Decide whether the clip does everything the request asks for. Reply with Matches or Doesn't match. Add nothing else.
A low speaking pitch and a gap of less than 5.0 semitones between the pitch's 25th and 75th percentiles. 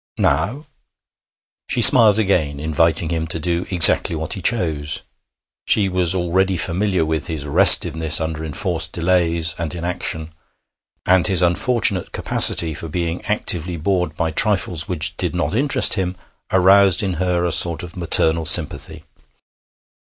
Matches